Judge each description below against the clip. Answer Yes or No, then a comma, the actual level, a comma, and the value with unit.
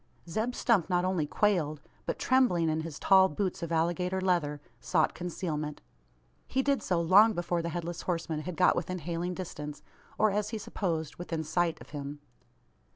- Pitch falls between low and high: Yes, medium, 175 Hz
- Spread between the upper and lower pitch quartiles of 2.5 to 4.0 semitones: Yes, average, 2.9 semitones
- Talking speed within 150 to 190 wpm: Yes, average, 170 wpm